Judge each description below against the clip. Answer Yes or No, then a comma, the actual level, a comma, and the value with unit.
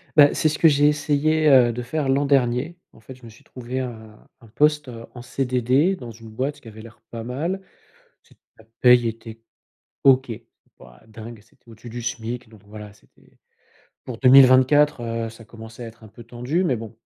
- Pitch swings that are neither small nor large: Yes, average, 3.5 semitones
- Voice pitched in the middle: No, low, 125 Hz